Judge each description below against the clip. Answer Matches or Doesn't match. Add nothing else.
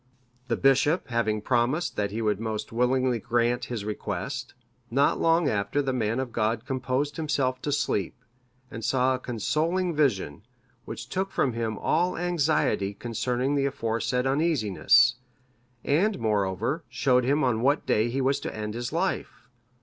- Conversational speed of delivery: Matches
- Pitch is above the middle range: Doesn't match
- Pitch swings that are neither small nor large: Matches